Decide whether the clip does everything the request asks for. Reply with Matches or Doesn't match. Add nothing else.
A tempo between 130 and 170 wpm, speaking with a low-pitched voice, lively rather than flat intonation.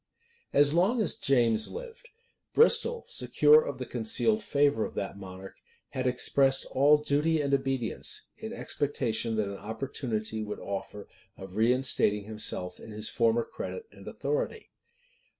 Matches